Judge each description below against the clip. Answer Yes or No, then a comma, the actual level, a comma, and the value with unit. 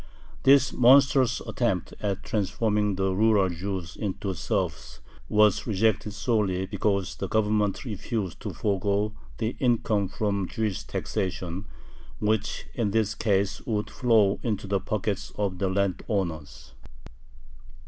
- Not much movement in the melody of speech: Yes, narrow, 2.3 semitones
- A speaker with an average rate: No, slow, 120 wpm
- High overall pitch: No, low, 100 Hz